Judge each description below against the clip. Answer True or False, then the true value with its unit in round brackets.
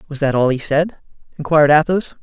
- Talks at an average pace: True (190 wpm)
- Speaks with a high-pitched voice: False (150 Hz)